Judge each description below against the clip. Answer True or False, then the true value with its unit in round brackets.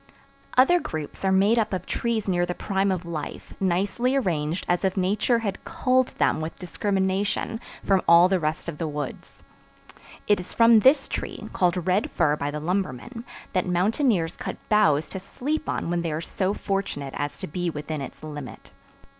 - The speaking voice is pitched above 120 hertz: True (185 Hz)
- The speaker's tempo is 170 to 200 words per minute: True (180 wpm)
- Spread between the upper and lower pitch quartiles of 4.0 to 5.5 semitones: True (4.4 semitones)